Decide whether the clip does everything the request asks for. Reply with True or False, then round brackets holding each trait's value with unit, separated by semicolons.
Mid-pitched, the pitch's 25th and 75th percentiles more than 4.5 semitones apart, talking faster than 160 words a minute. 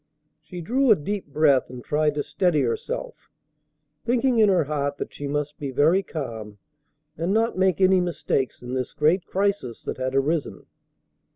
True (155 Hz; 5.5 semitones; 170 wpm)